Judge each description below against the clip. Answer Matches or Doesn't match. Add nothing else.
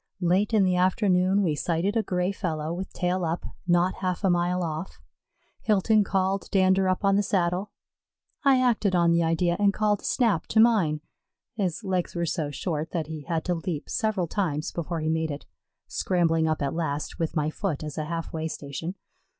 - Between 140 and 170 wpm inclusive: Doesn't match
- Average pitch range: Matches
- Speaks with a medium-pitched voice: Matches